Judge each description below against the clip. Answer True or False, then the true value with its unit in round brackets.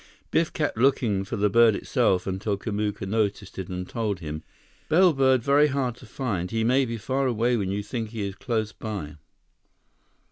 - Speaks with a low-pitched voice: True (110 Hz)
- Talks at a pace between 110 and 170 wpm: False (180 wpm)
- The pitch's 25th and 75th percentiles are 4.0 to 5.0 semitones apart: True (4.4 semitones)